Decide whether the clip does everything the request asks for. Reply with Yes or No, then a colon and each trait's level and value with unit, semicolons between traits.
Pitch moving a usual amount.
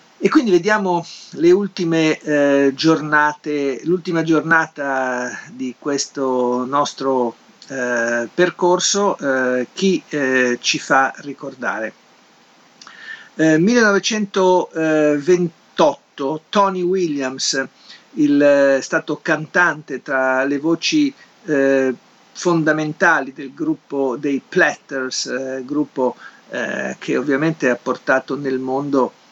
Yes: average, 4.9 semitones